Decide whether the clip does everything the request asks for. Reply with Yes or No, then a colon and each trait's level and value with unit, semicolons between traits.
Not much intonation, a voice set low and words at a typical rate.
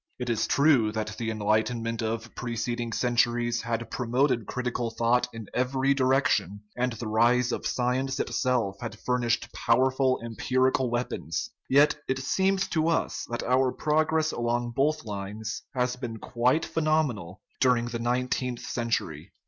Yes: narrow, 2.2 semitones; low, 120 Hz; average, 150 wpm